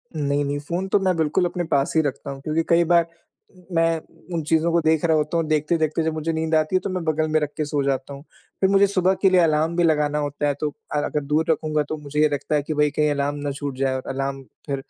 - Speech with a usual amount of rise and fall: No, narrow, 2.3 semitones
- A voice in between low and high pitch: Yes, medium, 155 Hz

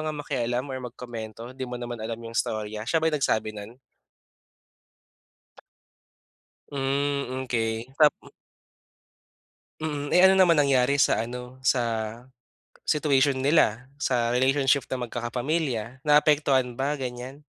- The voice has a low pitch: Yes, low, 130 Hz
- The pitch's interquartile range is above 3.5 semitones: No, average, 3.2 semitones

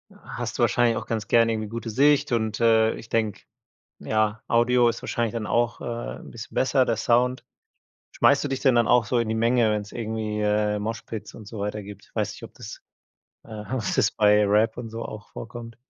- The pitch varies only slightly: Yes, narrow, 1.8 semitones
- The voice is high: No, low, 115 Hz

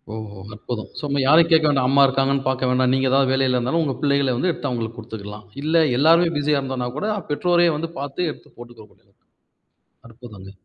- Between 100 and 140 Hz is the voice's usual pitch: Yes, low, 135 Hz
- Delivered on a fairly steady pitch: No, average, 3.7 semitones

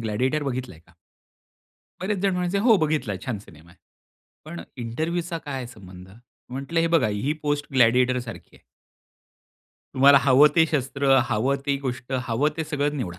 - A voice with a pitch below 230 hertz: Yes, low, 135 Hz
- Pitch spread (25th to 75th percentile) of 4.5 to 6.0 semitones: Yes, average, 4.8 semitones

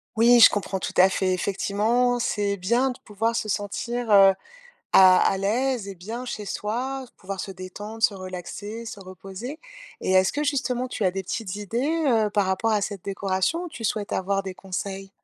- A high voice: Yes, high, 205 Hz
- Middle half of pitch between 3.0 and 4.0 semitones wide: Yes, average, 3.6 semitones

